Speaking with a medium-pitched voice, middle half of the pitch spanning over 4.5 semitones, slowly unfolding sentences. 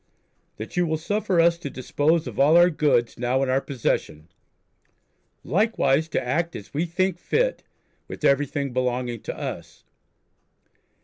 No: medium, 150 Hz; average, 5.0 semitones; average, 145 wpm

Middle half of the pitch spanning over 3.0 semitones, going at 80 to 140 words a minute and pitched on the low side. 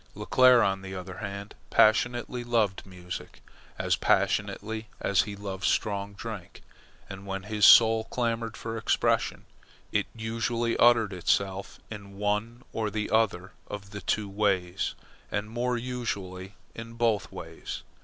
No: average, 2.7 semitones; slow, 135 wpm; low, 105 Hz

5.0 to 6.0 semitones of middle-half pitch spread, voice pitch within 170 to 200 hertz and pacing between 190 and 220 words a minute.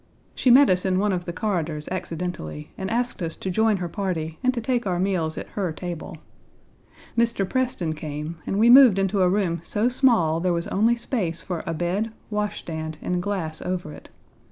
No: average, 4.3 semitones; medium, 185 Hz; average, 200 wpm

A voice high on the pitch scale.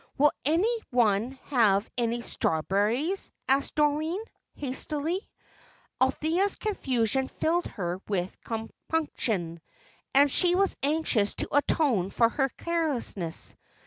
Yes: very high, 265 Hz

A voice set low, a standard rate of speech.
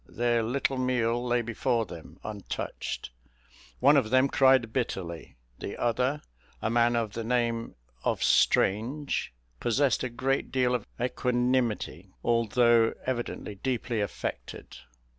No: low, 120 Hz; slow, 120 wpm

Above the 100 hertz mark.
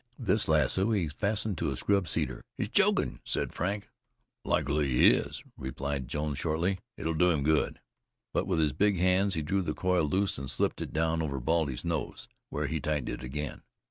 No: very low, 80 Hz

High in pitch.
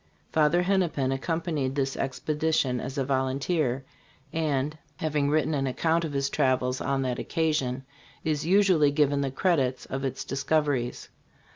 No: medium, 140 Hz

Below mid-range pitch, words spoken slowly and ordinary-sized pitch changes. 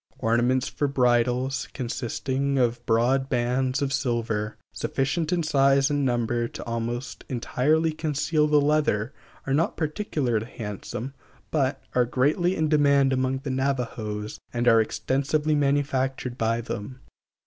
Yes: low, 130 Hz; slow, 130 wpm; average, 3.0 semitones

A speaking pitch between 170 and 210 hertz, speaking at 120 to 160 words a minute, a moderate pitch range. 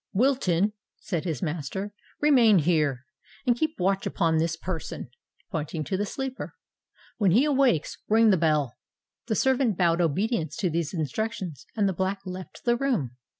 No: medium, 185 Hz; average, 150 wpm; wide, 5.9 semitones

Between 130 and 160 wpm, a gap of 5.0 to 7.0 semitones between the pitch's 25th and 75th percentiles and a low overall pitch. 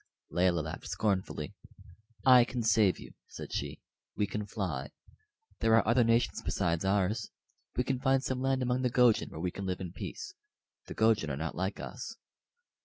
No: average, 180 wpm; average, 5.3 semitones; low, 105 Hz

